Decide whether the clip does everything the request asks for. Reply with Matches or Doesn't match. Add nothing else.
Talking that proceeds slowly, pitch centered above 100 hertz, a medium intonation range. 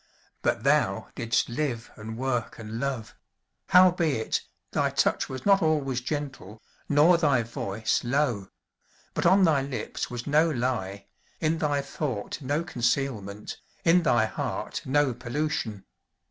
Matches